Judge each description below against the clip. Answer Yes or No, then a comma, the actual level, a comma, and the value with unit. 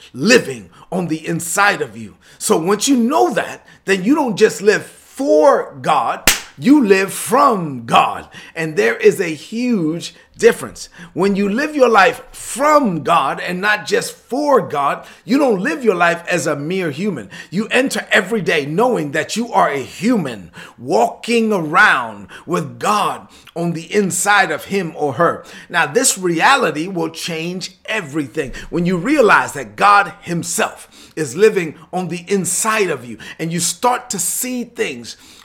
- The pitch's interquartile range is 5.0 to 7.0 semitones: Yes, average, 5.3 semitones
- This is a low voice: No, high, 195 Hz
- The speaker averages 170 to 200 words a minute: No, average, 160 wpm